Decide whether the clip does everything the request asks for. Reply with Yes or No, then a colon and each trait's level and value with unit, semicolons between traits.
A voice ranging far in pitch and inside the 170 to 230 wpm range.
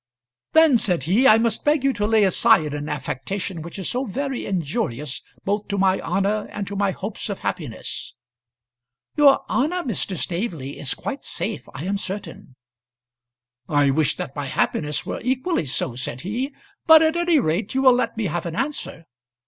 Yes: wide, 8.2 semitones; average, 180 wpm